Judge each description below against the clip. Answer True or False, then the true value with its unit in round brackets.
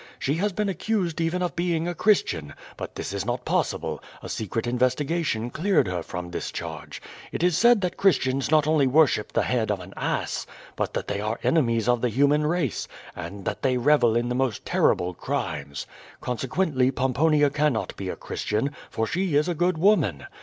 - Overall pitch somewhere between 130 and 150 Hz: True (135 Hz)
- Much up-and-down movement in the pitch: True (6.7 semitones)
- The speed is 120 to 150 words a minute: False (190 wpm)